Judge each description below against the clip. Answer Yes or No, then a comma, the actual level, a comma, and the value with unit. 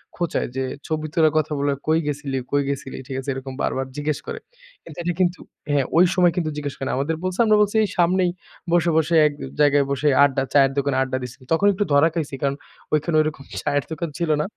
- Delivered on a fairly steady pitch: No, average, 3.4 semitones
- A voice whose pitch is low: No, medium, 150 Hz